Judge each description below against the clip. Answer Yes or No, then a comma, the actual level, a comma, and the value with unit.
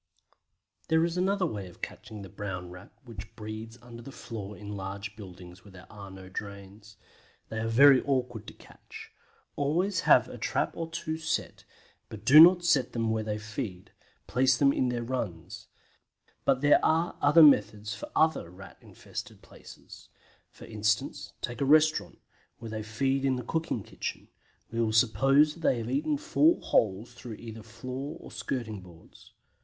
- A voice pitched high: No, low, 115 Hz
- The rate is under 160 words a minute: No, average, 170 wpm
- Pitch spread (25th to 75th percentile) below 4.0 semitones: No, average, 5.2 semitones